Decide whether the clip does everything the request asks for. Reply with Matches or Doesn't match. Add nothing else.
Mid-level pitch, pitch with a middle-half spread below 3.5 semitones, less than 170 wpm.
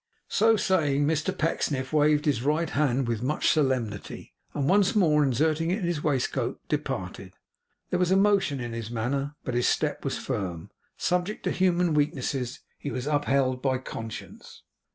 Doesn't match